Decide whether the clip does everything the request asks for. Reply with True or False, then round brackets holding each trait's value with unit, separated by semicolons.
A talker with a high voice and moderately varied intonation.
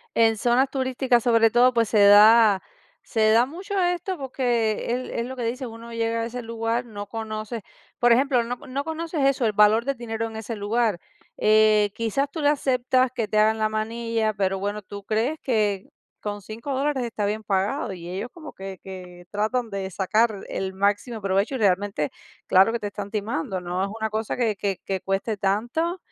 True (225 Hz; 3.3 semitones)